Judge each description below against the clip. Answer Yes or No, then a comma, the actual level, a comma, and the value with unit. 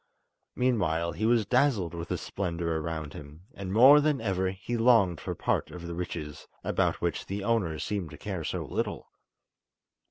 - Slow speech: No, average, 170 wpm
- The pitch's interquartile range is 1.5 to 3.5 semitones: No, wide, 5.4 semitones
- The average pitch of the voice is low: Yes, very low, 95 Hz